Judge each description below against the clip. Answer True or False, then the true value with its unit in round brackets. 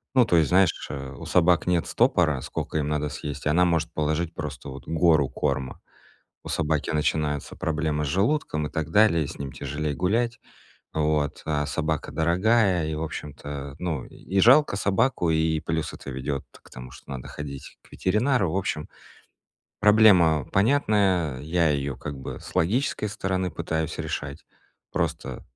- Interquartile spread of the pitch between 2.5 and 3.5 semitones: False (3.9 semitones)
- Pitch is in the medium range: False (80 Hz)